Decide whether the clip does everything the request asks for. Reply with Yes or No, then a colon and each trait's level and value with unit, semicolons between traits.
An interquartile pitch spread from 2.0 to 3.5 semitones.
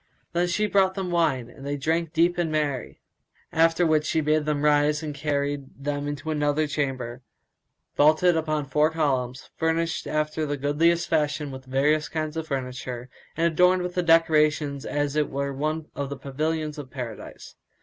Yes: narrow, 2.4 semitones